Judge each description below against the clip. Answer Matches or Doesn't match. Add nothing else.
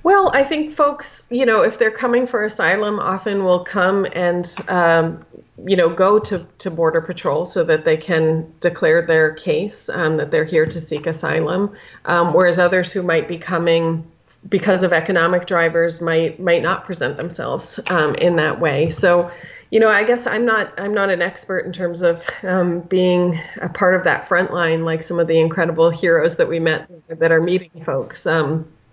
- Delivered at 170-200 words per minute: Matches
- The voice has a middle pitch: Matches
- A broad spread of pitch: Doesn't match